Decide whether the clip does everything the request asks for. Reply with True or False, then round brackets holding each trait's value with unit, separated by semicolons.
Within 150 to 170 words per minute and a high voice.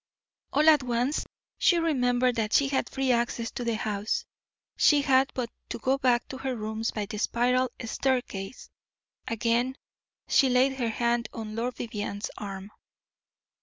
True (155 wpm; 245 Hz)